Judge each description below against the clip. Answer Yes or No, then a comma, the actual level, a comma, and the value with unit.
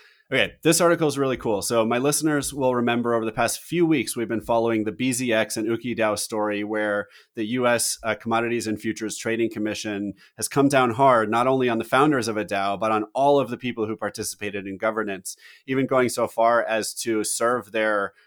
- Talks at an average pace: No, fast, 210 wpm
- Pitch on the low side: Yes, low, 115 Hz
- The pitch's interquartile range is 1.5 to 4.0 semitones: Yes, average, 2.9 semitones